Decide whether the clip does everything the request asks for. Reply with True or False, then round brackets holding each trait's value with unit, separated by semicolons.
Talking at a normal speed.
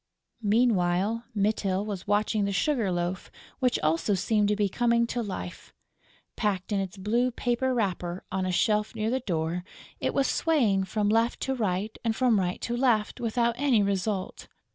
True (170 wpm)